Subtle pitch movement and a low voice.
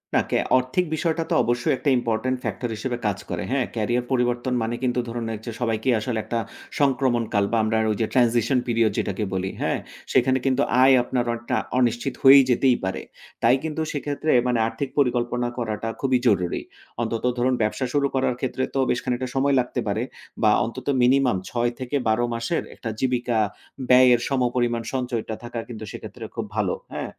Yes: narrow, 2.1 semitones; low, 120 Hz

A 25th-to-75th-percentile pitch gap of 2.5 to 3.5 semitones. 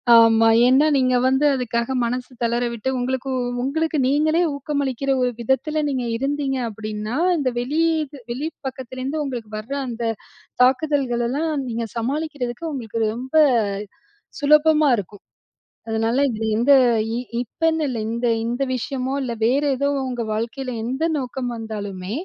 Yes: average, 3.2 semitones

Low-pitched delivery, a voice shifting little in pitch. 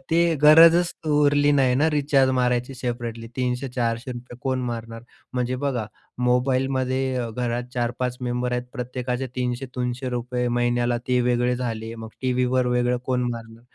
Yes: low, 125 Hz; narrow, 1.3 semitones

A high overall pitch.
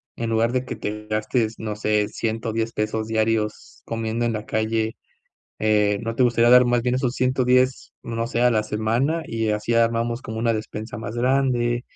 No: low, 115 Hz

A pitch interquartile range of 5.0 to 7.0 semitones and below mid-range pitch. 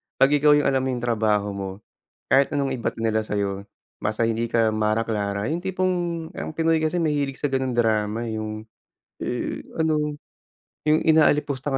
Yes: wide, 5.5 semitones; low, 120 Hz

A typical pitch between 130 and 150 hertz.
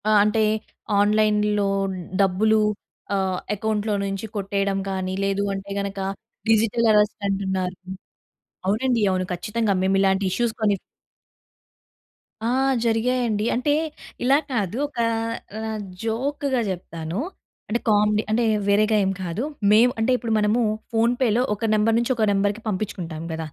No: high, 210 Hz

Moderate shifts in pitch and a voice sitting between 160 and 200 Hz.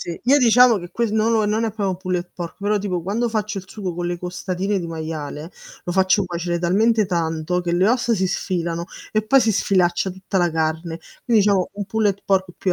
Yes: average, 3.5 semitones; high, 190 Hz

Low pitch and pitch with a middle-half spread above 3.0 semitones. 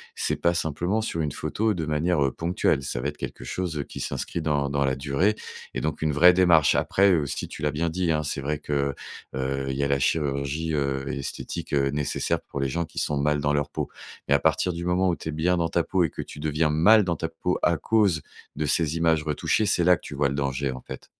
Yes: very low, 75 Hz; average, 3.4 semitones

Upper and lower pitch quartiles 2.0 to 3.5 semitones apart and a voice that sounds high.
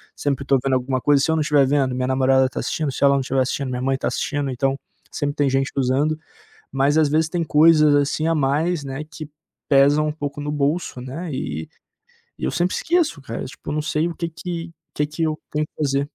No: narrow, 2.4 semitones; medium, 145 Hz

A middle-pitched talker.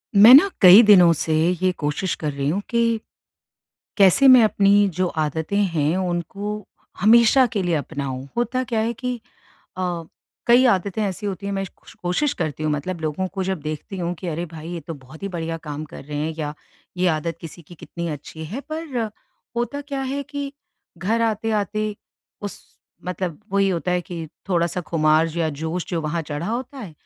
Yes: medium, 180 Hz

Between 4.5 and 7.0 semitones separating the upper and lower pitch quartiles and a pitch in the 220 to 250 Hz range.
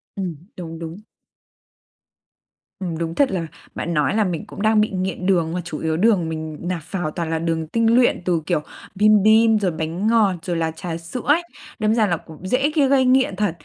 No: average, 4.8 semitones; medium, 185 Hz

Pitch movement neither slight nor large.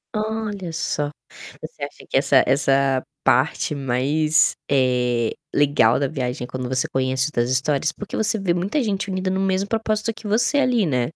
No: wide, 7.4 semitones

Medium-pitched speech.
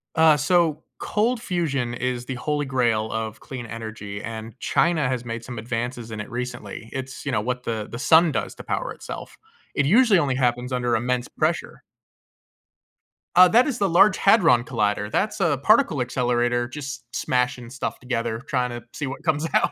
No: low, 125 Hz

